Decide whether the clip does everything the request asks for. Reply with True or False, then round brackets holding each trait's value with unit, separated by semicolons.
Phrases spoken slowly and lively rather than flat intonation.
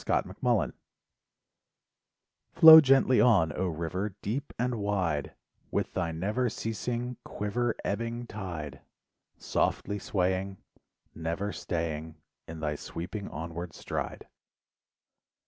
True (100 wpm; 5.9 semitones)